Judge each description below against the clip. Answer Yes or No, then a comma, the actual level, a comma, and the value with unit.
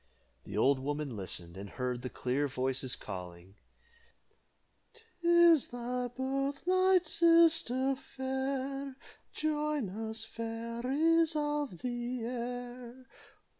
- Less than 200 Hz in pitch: No, very high, 250 Hz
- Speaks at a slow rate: Yes, slow, 95 wpm